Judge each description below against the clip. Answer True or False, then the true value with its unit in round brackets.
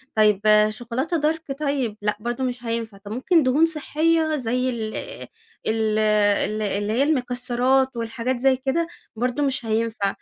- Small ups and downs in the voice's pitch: False (3.8 semitones)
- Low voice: False (245 Hz)